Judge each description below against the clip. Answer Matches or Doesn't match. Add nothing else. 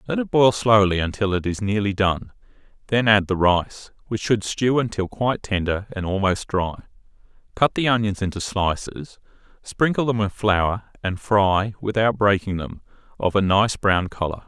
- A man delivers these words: Matches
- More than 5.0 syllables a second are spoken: Doesn't match